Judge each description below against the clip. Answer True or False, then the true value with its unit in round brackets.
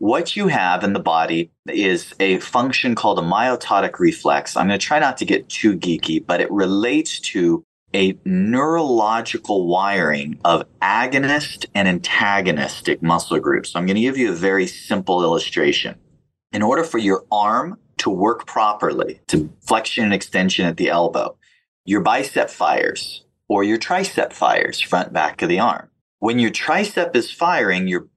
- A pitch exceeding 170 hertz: False (105 Hz)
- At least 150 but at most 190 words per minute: True (170 wpm)